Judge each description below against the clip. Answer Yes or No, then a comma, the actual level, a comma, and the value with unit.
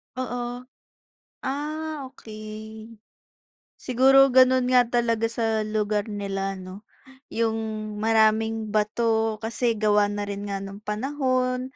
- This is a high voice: Yes, high, 225 Hz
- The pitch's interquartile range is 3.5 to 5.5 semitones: No, average, 3.1 semitones